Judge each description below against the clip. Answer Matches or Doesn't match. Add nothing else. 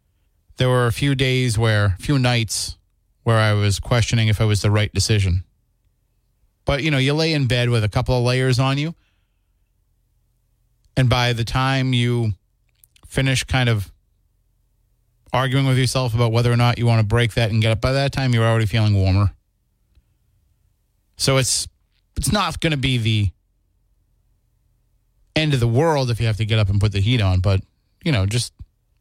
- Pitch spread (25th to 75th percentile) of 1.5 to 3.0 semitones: Doesn't match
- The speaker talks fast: Doesn't match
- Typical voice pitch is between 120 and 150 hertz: Doesn't match